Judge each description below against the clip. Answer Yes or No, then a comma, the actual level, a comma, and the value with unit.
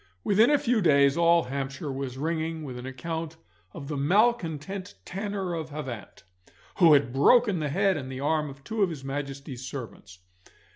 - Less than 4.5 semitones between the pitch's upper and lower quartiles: No, average, 4.8 semitones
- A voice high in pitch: No, medium, 155 Hz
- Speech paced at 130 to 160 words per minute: No, average, 175 wpm